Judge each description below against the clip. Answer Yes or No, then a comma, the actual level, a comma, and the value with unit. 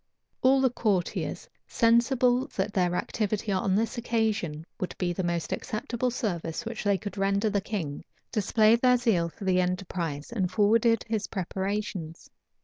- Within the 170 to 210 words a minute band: No, average, 150 wpm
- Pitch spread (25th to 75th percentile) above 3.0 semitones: Yes, average, 4.0 semitones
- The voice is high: Yes, high, 205 Hz